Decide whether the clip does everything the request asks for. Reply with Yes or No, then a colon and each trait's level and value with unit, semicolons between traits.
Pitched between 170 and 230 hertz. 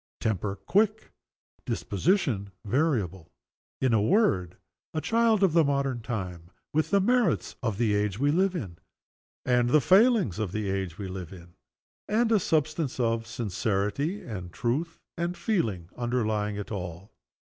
No: low, 120 Hz